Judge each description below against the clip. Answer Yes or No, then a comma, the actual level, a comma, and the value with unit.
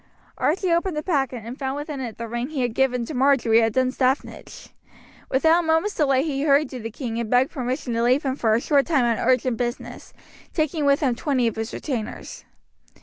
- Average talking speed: No, fast, 210 wpm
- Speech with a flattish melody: No, average, 3.6 semitones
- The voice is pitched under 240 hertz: No, very high, 265 Hz